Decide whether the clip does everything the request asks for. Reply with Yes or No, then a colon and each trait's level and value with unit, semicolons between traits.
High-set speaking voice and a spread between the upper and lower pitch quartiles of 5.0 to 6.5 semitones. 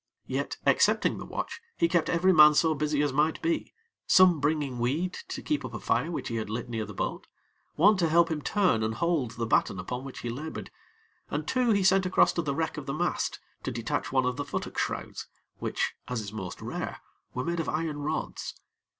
No: medium, 150 Hz; wide, 5.4 semitones